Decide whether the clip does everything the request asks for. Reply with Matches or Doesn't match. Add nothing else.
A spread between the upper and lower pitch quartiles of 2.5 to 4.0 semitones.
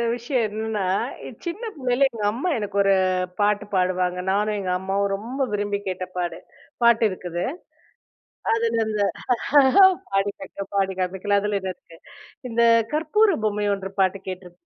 Matches